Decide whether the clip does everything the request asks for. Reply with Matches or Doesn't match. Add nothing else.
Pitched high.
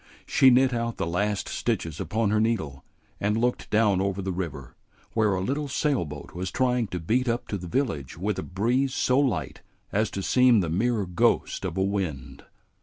Doesn't match